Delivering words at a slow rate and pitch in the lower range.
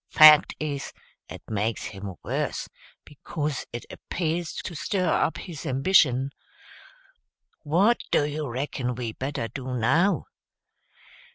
No: slow, 115 wpm; medium, 145 Hz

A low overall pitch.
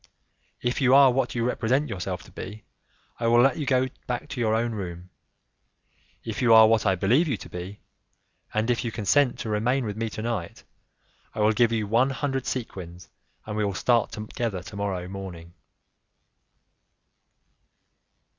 Yes: low, 115 Hz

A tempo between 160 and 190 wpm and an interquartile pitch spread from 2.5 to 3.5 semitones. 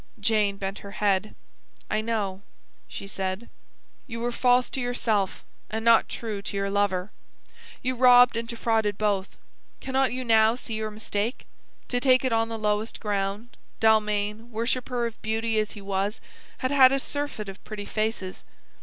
Yes: average, 165 wpm; average, 2.9 semitones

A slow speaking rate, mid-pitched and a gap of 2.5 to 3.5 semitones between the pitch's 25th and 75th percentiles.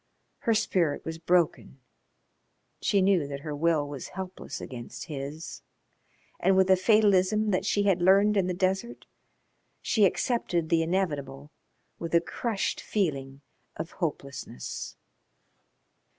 No: slow, 125 wpm; medium, 175 Hz; average, 4.5 semitones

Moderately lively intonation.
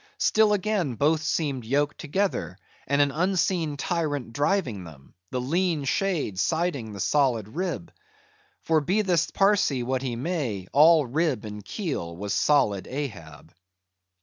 No: wide, 6.8 semitones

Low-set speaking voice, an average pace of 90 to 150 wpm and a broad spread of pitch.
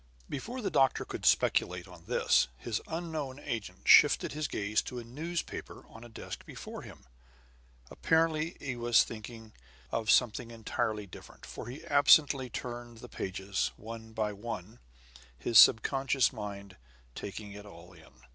No: low, 115 Hz; average, 145 wpm; average, 4.5 semitones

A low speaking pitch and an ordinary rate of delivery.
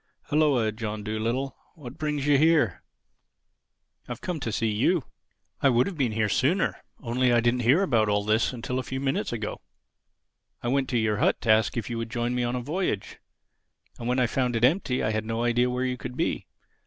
No: low, 125 Hz; fast, 215 wpm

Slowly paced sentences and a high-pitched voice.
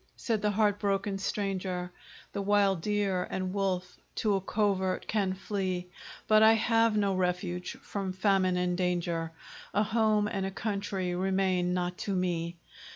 No: average, 155 wpm; high, 195 Hz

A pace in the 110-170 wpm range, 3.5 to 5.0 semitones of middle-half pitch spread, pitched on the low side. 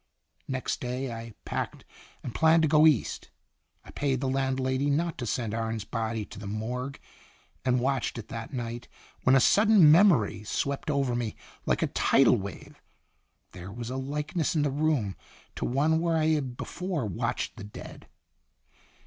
Yes: average, 165 wpm; average, 4.6 semitones; low, 130 Hz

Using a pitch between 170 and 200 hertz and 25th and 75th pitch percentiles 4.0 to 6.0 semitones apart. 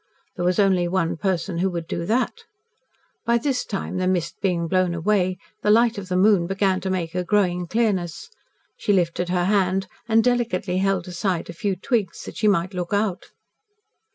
No: medium, 185 Hz; average, 2.7 semitones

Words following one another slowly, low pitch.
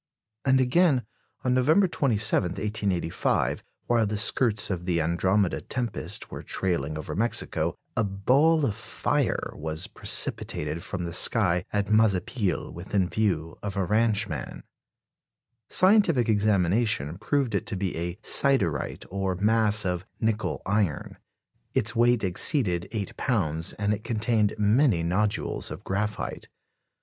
Yes: slow, 130 wpm; low, 105 Hz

